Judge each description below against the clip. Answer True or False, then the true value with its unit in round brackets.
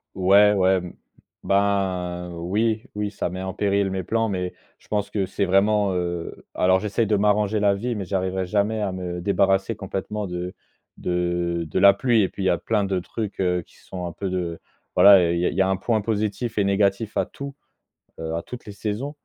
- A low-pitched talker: True (100 Hz)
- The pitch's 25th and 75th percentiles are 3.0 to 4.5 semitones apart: False (2.4 semitones)